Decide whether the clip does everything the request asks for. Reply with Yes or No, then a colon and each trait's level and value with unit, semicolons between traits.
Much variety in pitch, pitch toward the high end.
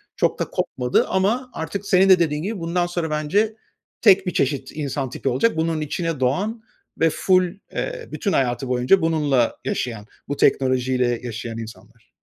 No: wide, 6.6 semitones; medium, 155 Hz